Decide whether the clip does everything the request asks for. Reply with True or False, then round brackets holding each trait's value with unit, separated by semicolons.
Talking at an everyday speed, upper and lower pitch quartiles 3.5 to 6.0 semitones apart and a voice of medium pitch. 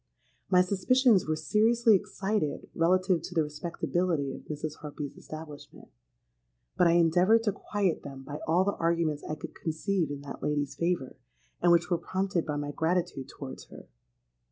True (160 wpm; 3.8 semitones; 165 Hz)